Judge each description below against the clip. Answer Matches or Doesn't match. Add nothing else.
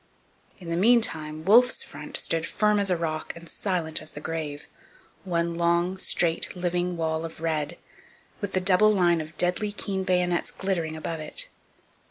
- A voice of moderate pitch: Matches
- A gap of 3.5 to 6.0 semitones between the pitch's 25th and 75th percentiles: Doesn't match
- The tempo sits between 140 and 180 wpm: Matches